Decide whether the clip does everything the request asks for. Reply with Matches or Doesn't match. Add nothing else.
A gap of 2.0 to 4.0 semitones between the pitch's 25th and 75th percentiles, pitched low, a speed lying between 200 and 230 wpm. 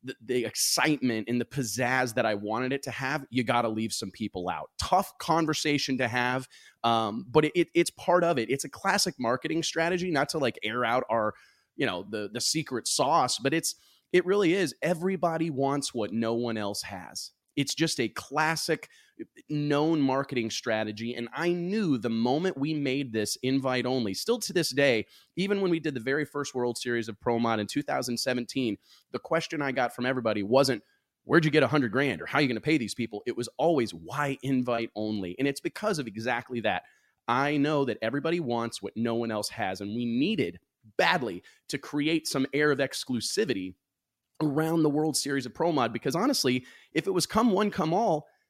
Doesn't match